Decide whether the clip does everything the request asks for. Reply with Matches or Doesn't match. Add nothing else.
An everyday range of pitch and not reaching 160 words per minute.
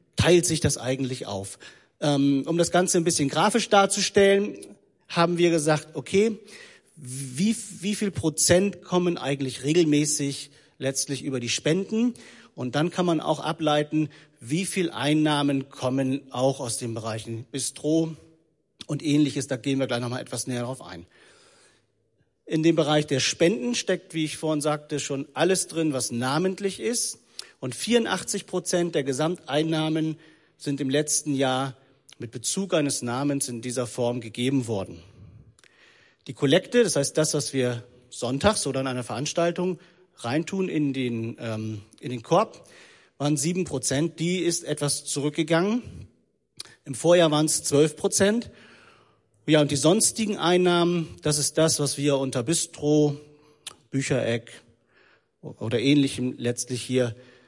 Matches